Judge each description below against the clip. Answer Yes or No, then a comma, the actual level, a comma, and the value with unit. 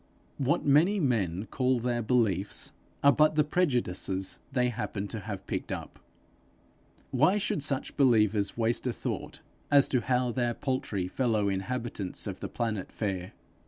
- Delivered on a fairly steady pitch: No, average, 4.7 semitones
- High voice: No, low, 120 Hz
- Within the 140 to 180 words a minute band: Yes, average, 150 wpm